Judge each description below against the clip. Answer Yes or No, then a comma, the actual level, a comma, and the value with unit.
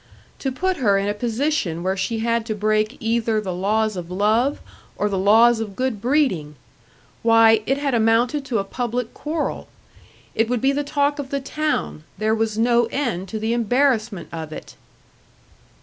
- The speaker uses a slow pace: No, average, 180 wpm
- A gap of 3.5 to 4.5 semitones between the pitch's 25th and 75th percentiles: Yes, average, 4.0 semitones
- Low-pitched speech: No, high, 225 Hz